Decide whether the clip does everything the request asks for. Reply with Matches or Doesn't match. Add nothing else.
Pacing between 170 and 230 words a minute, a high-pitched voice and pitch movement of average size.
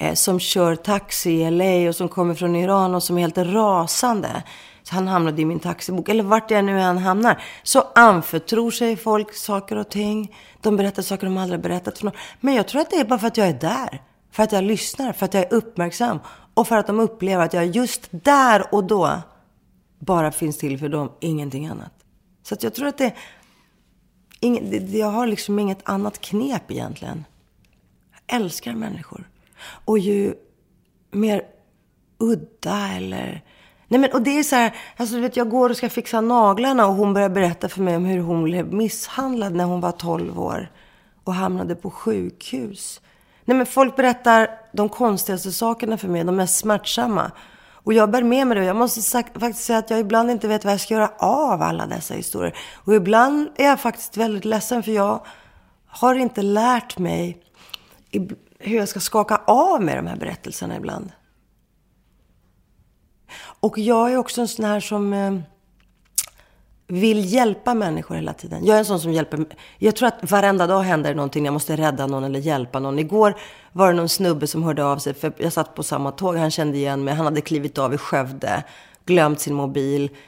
Matches